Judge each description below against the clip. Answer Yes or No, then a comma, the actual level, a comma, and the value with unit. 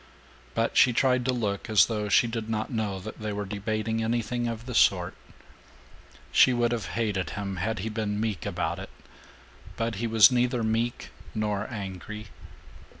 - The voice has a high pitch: No, low, 110 Hz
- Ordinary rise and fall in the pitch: No, narrow, 2.2 semitones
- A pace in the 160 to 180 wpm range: Yes, average, 170 wpm